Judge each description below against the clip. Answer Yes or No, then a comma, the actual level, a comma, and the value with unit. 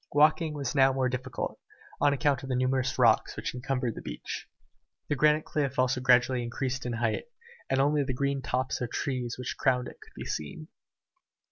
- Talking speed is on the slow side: No, average, 195 wpm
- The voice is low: Yes, low, 130 Hz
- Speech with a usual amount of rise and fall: No, narrow, 1.9 semitones